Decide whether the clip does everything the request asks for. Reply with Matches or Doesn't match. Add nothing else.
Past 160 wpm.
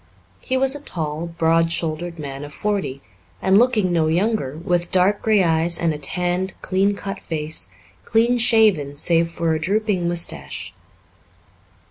Doesn't match